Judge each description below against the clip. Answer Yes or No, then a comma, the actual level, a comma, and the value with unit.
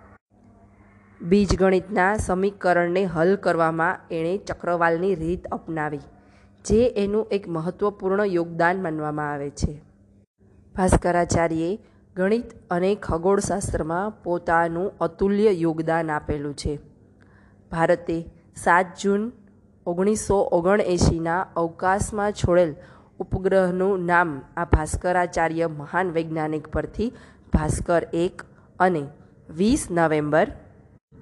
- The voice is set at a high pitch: No, medium, 175 Hz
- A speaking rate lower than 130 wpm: Yes, average, 85 wpm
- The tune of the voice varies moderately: Yes, average, 3.2 semitones